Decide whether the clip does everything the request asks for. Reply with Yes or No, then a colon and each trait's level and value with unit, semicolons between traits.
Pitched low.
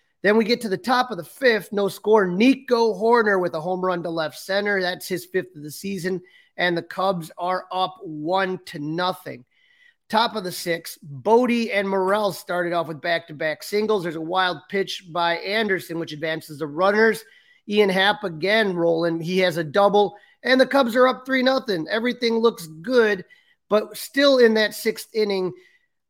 No: high, 195 Hz